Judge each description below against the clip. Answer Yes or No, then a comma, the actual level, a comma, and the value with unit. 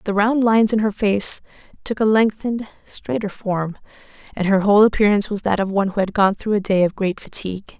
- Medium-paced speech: No, fast, 215 wpm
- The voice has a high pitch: Yes, high, 205 Hz